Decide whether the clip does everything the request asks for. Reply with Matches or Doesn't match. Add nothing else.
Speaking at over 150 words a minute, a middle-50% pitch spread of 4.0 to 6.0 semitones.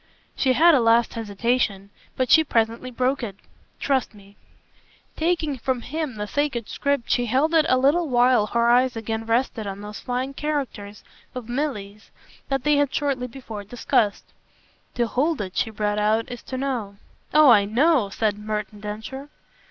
Matches